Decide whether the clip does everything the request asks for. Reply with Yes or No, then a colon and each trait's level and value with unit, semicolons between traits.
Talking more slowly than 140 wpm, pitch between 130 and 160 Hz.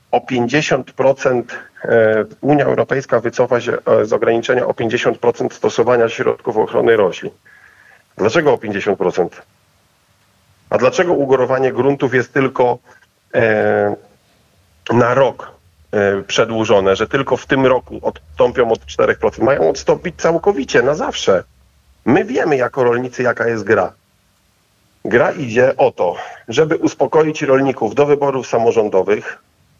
Yes: average, 115 wpm; low, 135 Hz